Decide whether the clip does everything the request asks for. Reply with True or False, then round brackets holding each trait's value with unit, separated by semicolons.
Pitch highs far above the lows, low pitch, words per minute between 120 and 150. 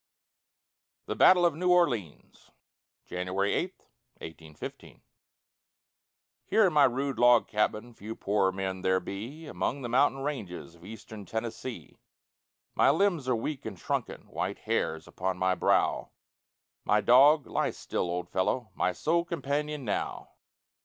True (7.5 semitones; 115 Hz; 135 wpm)